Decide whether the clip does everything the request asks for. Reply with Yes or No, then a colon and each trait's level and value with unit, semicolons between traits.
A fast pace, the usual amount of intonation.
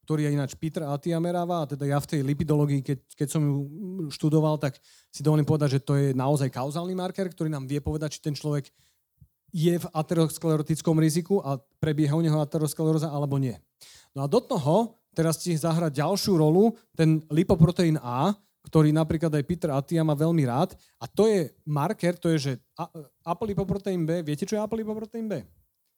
Yes: fast, 180 wpm; average, 3.2 semitones